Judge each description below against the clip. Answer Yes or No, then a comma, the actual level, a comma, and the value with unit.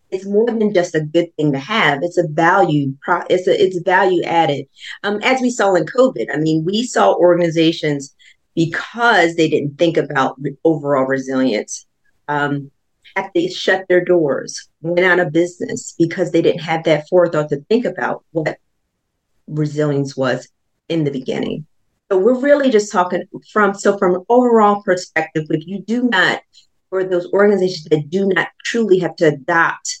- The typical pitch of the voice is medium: Yes, medium, 175 Hz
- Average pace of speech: Yes, average, 170 wpm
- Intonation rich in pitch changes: No, average, 4.7 semitones